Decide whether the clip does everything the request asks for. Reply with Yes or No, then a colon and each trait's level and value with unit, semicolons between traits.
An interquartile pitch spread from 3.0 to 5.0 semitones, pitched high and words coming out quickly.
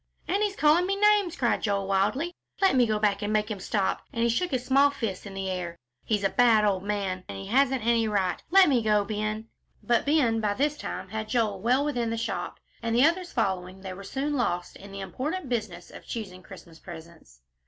No: wide, 5.4 semitones; high, 220 Hz; fast, 225 wpm